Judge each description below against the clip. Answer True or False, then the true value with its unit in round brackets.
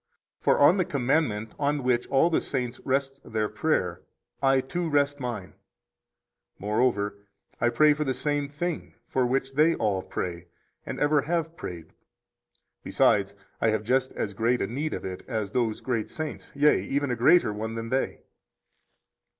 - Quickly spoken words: False (165 wpm)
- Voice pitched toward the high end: False (130 Hz)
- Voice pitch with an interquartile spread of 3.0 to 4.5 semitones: False (4.9 semitones)